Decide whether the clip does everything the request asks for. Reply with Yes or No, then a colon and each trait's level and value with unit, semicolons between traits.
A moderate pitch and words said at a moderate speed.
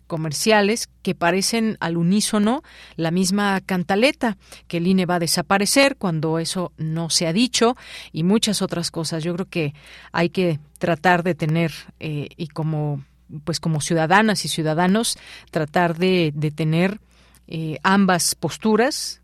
Yes: medium, 175 Hz; average, 145 wpm